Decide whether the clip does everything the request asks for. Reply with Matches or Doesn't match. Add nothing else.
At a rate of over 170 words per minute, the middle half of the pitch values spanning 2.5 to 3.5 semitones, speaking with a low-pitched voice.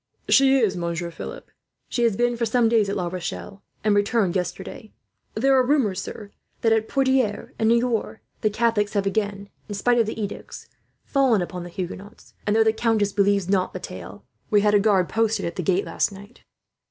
Doesn't match